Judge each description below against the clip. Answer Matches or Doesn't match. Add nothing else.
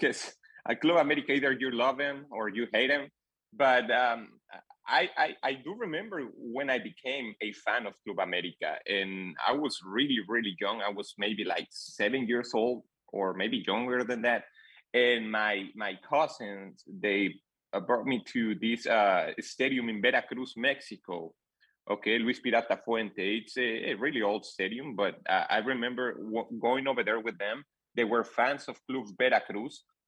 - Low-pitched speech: Matches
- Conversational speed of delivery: Matches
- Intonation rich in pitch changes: Doesn't match